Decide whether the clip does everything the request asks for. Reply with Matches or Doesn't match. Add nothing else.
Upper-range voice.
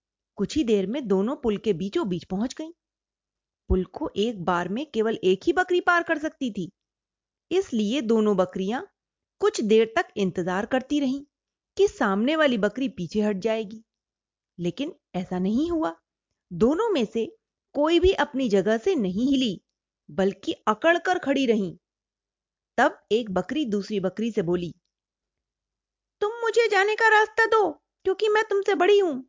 Matches